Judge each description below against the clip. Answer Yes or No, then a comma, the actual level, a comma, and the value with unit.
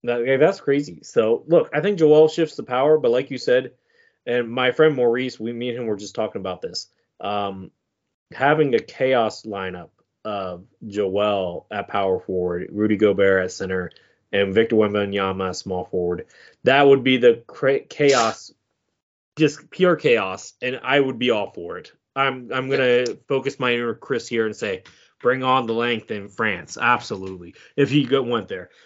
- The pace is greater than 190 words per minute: No, average, 175 wpm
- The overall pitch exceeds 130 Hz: No, low, 120 Hz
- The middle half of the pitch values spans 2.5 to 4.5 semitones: No, wide, 5.6 semitones